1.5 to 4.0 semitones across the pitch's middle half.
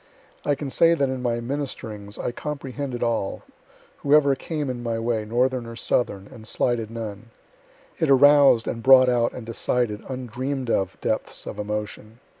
Yes: average, 3.1 semitones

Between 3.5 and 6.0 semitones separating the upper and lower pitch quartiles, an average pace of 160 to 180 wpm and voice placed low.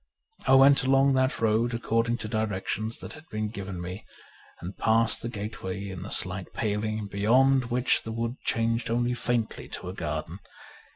No: average, 2.8 semitones; average, 170 wpm; low, 115 Hz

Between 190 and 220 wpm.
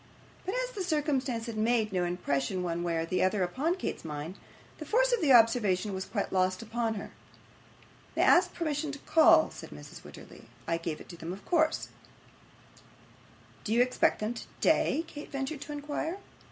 No: average, 175 wpm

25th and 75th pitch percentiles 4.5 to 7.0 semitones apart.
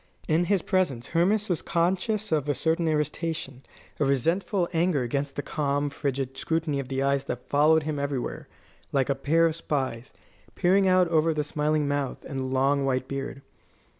No: average, 3.4 semitones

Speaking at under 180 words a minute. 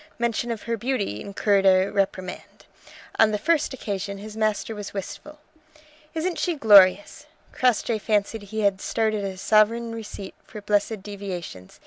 Yes: average, 145 wpm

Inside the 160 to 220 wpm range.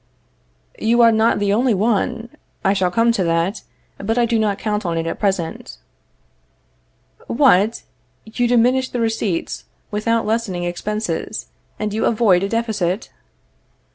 No: average, 140 wpm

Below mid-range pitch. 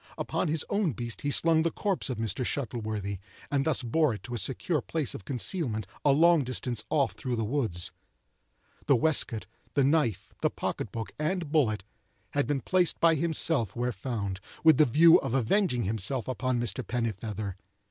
Yes: low, 130 Hz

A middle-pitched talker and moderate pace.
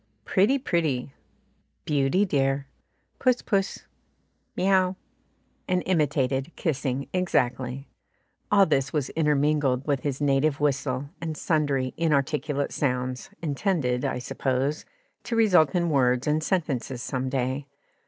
No: medium, 145 Hz; slow, 115 wpm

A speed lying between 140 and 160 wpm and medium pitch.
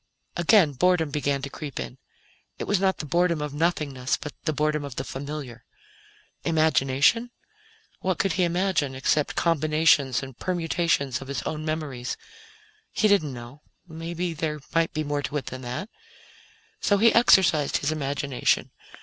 Yes: average, 155 wpm; medium, 155 Hz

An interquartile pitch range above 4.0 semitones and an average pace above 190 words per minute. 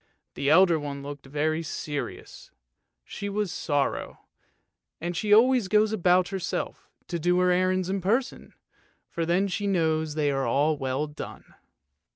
No: average, 4.4 semitones; average, 145 wpm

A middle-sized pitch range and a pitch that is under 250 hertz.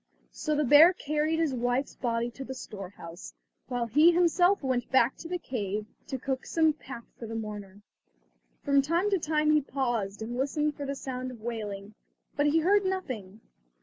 No: average, 5.0 semitones; very high, 265 Hz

